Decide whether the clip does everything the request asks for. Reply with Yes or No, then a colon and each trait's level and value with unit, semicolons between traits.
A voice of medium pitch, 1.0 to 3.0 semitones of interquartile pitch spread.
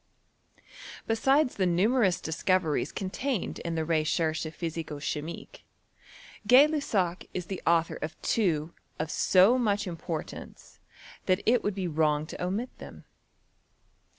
No: medium, 180 Hz; average, 4.5 semitones